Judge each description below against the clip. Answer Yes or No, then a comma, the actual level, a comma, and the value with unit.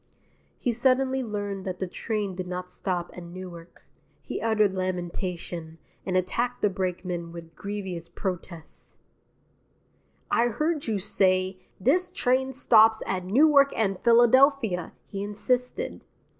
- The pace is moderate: No, slow, 125 wpm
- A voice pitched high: Yes, high, 195 Hz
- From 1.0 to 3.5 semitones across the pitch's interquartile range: No, average, 4.9 semitones